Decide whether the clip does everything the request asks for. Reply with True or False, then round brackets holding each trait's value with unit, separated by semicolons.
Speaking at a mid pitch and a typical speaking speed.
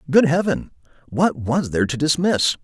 True (150 Hz; 160 wpm)